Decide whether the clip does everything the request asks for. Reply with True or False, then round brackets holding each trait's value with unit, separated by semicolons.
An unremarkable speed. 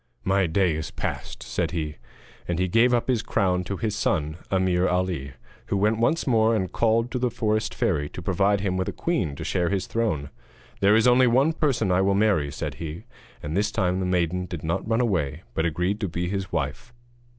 False (215 wpm)